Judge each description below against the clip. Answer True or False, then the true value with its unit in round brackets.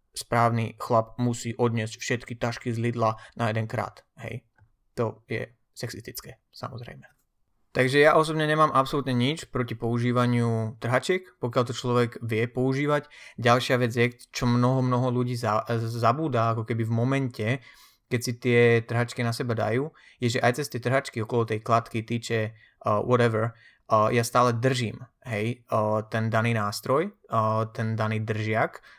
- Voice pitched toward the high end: False (120 Hz)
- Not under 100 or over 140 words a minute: False (155 wpm)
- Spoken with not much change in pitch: True (1.9 semitones)